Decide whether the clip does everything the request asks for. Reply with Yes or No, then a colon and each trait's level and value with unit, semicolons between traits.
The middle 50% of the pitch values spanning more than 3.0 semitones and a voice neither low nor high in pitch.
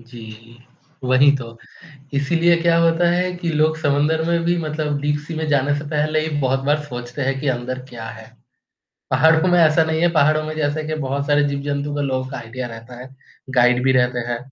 Yes: average, 3.6 semitones; medium, 145 Hz